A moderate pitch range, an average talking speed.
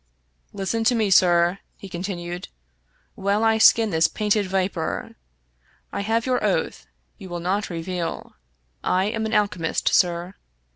Yes: average, 3.4 semitones; average, 150 wpm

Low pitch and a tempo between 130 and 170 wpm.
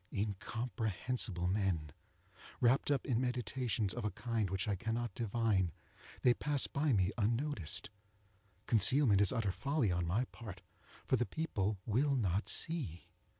Yes: low, 110 Hz; average, 140 wpm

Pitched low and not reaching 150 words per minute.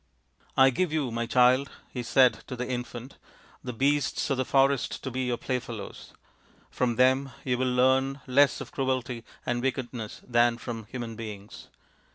No: low, 125 Hz; average, 180 wpm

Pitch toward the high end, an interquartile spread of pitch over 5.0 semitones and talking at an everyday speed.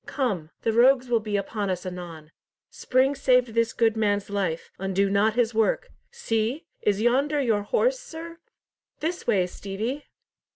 No: high, 225 Hz; average, 4.6 semitones; average, 155 wpm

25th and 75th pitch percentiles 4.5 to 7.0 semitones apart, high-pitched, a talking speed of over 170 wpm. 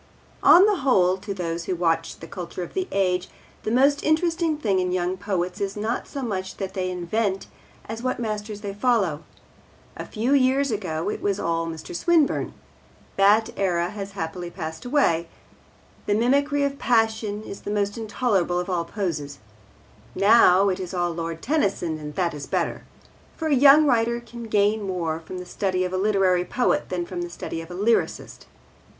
Yes: average, 4.8 semitones; high, 195 Hz; average, 180 wpm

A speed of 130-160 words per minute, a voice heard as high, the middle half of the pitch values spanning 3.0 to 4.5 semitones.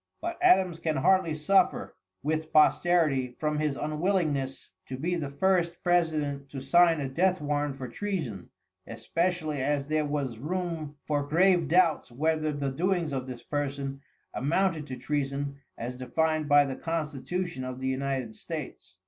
No: average, 150 wpm; medium, 150 Hz; average, 3.6 semitones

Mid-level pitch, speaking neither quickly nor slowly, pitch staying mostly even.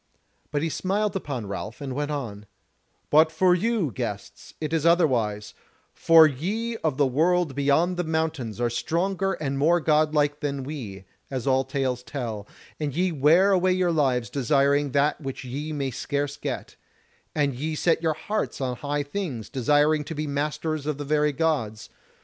No: medium, 145 Hz; average, 170 wpm; average, 3.3 semitones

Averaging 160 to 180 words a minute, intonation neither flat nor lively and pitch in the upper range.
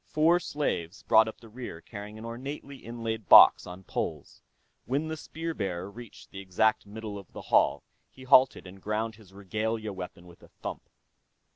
No: average, 175 wpm; average, 3.9 semitones; low, 110 Hz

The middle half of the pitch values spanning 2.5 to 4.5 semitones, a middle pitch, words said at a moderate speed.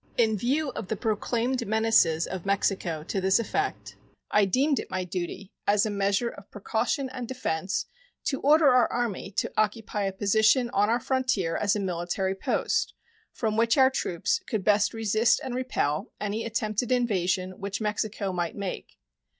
No: average, 3.7 semitones; high, 210 Hz; average, 165 wpm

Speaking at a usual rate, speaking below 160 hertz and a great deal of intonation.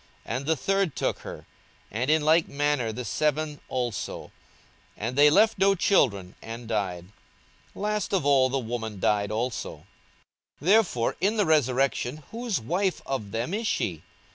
Yes: average, 165 wpm; low, 135 Hz; wide, 7.7 semitones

